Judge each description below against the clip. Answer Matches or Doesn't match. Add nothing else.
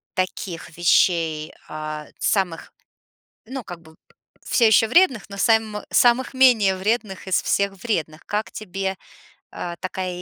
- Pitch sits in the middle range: Doesn't match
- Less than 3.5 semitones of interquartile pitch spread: Doesn't match